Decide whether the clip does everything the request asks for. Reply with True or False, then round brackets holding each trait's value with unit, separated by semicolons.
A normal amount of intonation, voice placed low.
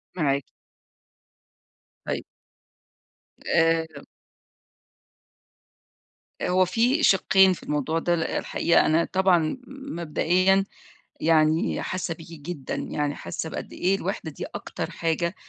False (3.0 semitones; 170 Hz)